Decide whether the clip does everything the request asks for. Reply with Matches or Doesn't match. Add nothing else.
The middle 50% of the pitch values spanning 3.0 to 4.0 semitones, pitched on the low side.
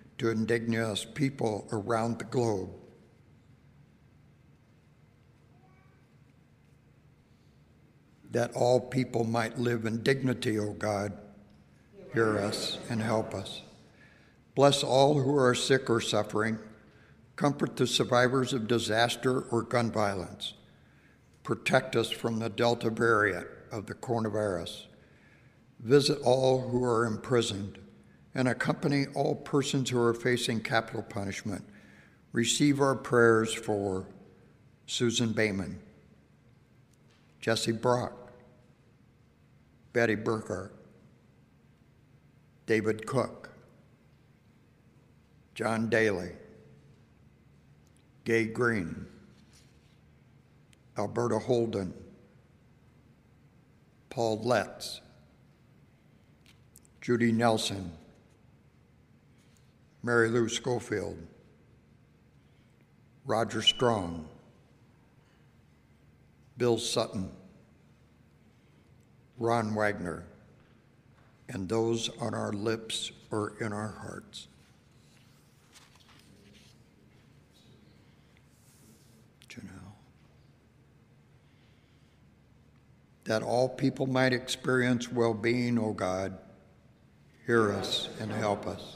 Doesn't match